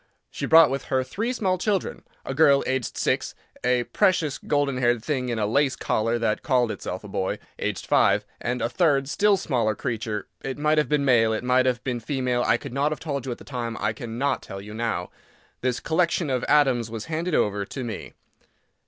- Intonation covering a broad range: No, average, 4.2 semitones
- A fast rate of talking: Yes, fast, 210 wpm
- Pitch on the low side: Yes, low, 130 Hz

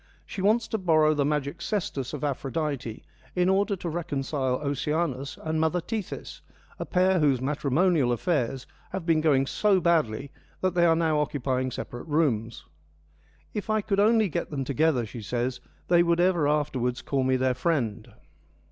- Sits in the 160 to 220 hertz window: No, medium, 150 Hz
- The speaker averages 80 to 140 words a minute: No, average, 170 wpm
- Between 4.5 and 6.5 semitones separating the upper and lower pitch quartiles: Yes, average, 4.9 semitones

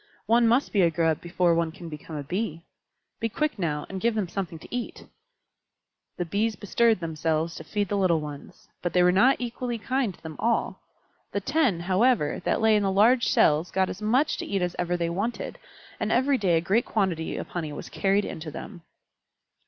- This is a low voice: No, high, 190 Hz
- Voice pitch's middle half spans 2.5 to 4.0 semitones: No, average, 5.2 semitones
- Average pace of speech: No, fast, 210 wpm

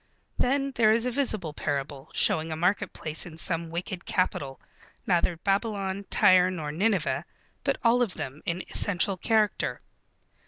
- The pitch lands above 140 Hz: Yes, medium, 185 Hz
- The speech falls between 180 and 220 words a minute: No, average, 145 wpm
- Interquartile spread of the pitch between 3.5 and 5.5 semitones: Yes, average, 4.9 semitones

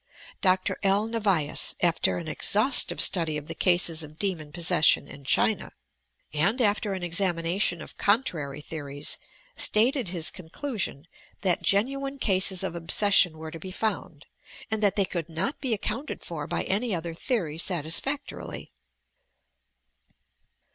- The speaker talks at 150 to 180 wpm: No, average, 140 wpm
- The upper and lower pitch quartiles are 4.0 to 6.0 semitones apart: Yes, average, 4.5 semitones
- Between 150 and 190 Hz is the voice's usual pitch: Yes, medium, 185 Hz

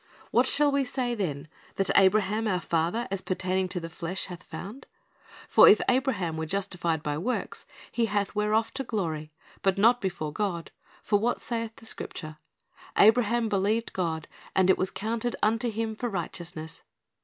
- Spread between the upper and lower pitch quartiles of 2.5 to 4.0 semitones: No, average, 4.6 semitones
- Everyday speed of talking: Yes, average, 165 wpm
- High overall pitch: Yes, high, 200 Hz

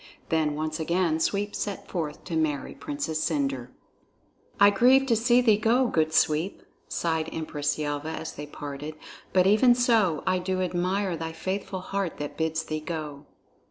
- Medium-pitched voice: Yes, medium, 165 Hz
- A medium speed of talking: Yes, average, 160 wpm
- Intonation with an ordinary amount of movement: Yes, average, 4.4 semitones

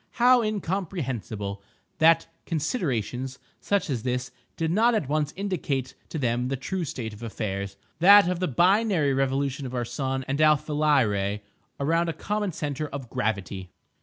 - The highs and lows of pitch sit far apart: Yes, wide, 5.8 semitones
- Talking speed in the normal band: Yes, average, 150 wpm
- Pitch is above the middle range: No, medium, 140 Hz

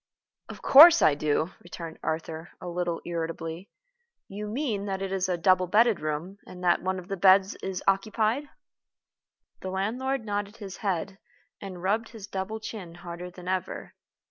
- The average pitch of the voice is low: No, high, 190 Hz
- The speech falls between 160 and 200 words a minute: Yes, average, 170 wpm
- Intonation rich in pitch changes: No, average, 3.0 semitones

